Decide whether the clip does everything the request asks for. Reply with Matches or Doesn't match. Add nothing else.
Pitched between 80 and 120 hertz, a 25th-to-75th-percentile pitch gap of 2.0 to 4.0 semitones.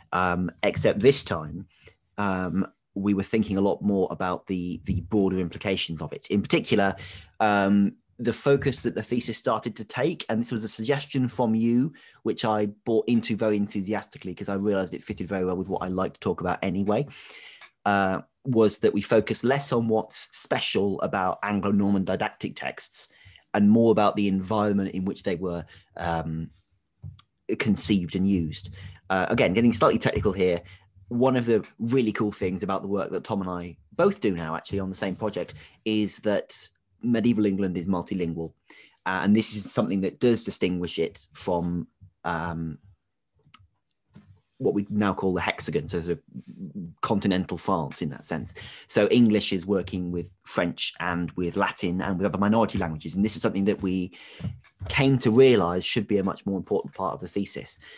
Matches